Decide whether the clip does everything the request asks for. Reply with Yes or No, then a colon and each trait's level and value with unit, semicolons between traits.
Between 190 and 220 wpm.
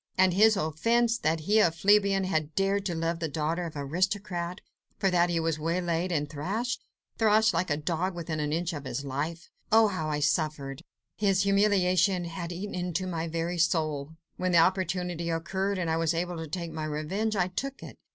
Yes: average, 200 wpm